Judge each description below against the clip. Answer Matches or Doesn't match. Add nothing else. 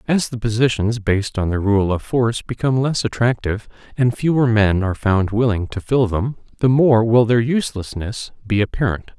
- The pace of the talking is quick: Doesn't match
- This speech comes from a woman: Doesn't match